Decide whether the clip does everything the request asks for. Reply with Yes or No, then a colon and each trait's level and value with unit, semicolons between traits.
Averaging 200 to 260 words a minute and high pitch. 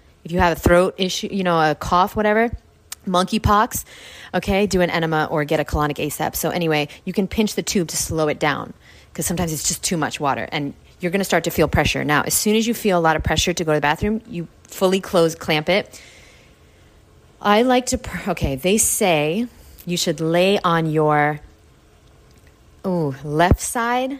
No: fast, 205 wpm; medium, 175 Hz